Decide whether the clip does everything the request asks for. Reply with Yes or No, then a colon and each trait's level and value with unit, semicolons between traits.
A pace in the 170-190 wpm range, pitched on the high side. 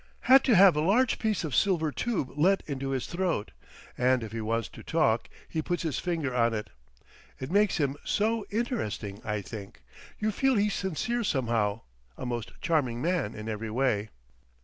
No: average, 180 wpm; medium, 145 Hz